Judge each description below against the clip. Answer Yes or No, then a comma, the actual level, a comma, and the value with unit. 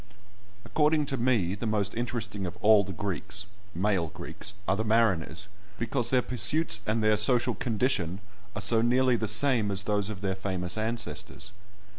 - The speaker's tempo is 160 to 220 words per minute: Yes, average, 165 wpm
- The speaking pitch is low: Yes, low, 110 Hz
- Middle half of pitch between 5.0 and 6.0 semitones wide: No, average, 3.4 semitones